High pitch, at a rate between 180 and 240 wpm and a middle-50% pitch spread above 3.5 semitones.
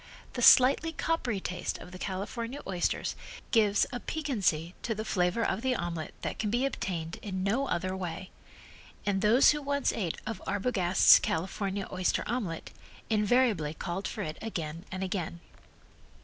No: high, 200 Hz; average, 155 wpm; average, 4.9 semitones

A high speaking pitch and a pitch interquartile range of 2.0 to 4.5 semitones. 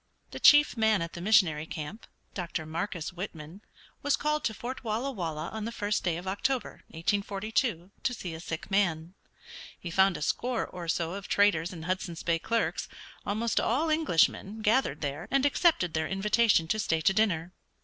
No: high, 195 Hz; average, 4.9 semitones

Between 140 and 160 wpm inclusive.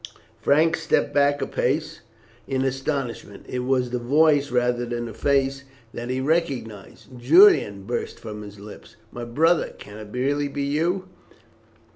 Yes: average, 150 wpm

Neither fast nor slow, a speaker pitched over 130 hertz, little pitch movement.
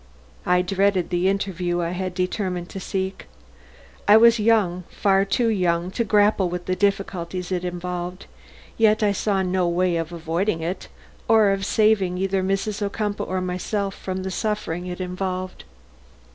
Yes: average, 160 wpm; medium, 185 Hz; narrow, 2.0 semitones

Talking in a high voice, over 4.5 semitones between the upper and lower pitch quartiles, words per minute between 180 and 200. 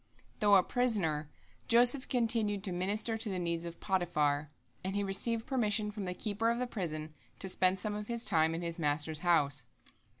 Yes: high, 195 Hz; average, 5.1 semitones; average, 190 wpm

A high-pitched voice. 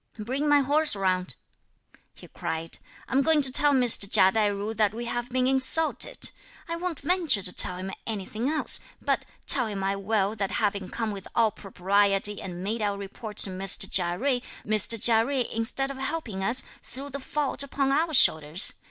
Yes: high, 225 Hz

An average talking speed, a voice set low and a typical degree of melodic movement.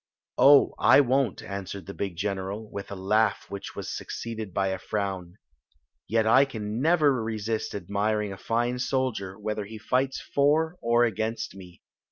Yes: average, 165 wpm; low, 110 Hz; average, 3.6 semitones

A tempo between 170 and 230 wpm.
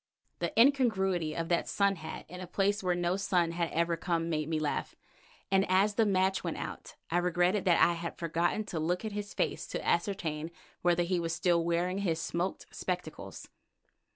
Yes: average, 190 wpm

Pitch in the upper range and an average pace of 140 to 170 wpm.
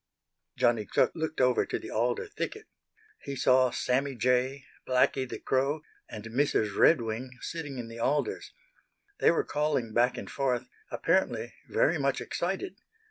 No: low, 130 Hz; average, 145 wpm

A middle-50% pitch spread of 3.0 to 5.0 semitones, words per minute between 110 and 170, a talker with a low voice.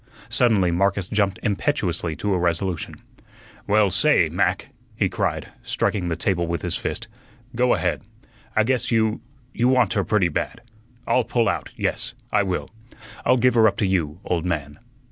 Yes: average, 4.5 semitones; average, 165 wpm; low, 100 Hz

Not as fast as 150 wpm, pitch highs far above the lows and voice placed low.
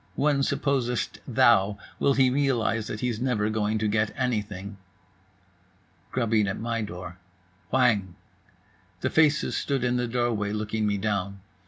No: average, 140 wpm; average, 3.2 semitones; low, 110 Hz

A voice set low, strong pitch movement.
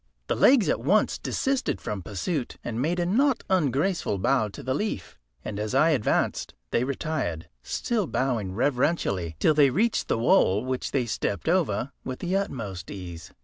Yes: low, 130 Hz; wide, 8.7 semitones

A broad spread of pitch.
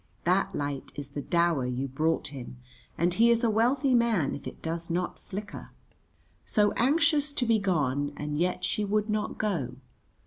Yes: wide, 7.3 semitones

